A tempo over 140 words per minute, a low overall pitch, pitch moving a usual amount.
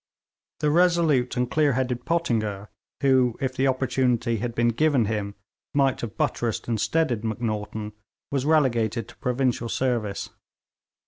No: slow, 135 wpm; low, 125 Hz; average, 3.3 semitones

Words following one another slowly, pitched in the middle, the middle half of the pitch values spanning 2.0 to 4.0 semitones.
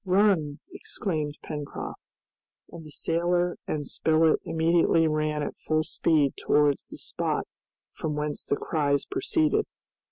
Yes: slow, 125 wpm; medium, 155 Hz; narrow, 2.6 semitones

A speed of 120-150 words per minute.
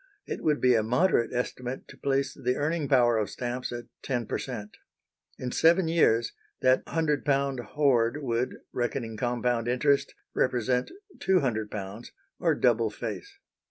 Yes: average, 140 wpm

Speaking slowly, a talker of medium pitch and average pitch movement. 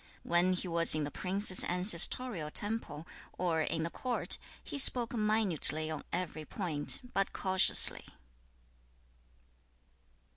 Yes: slow, 120 wpm; medium, 180 Hz; average, 4.4 semitones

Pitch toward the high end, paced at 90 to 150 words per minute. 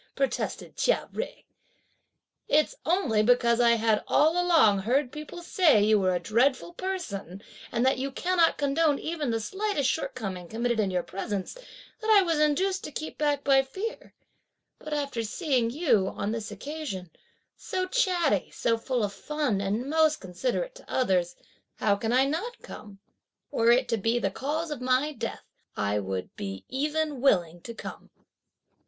No: very high, 260 Hz; average, 165 wpm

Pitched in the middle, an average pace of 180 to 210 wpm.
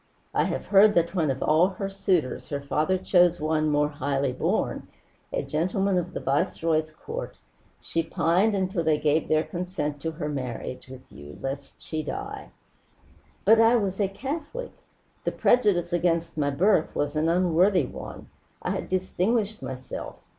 No: medium, 170 Hz; average, 160 wpm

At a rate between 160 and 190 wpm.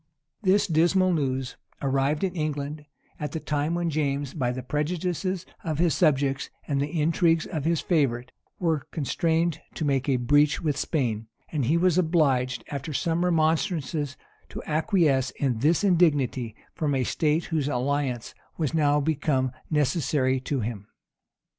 No: average, 150 wpm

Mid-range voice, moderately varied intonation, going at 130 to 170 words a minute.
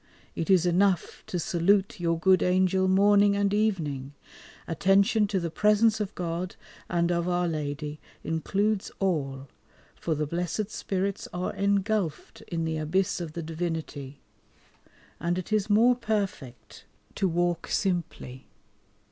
Yes: medium, 180 Hz; average, 3.5 semitones; slow, 135 wpm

